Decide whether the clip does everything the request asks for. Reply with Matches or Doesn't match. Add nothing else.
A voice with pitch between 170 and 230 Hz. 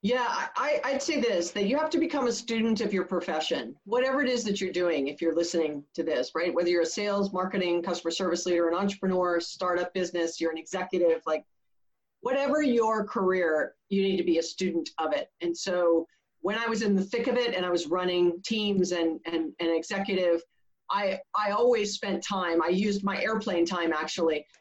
Matches